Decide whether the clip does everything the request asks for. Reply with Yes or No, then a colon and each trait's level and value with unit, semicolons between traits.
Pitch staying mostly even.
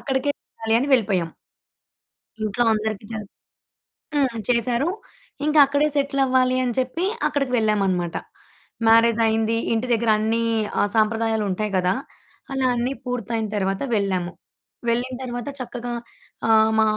No: average, 3.0 semitones